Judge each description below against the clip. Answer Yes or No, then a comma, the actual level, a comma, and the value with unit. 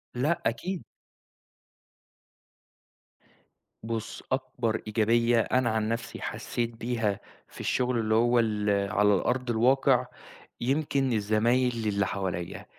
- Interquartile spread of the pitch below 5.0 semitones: Yes, narrow, 2.5 semitones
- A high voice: No, low, 115 Hz